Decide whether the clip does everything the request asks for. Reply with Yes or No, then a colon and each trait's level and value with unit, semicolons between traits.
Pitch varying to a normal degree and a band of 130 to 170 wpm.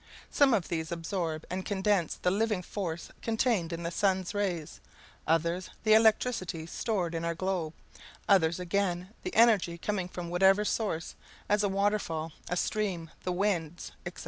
Yes: average, 3.5 semitones; average, 155 wpm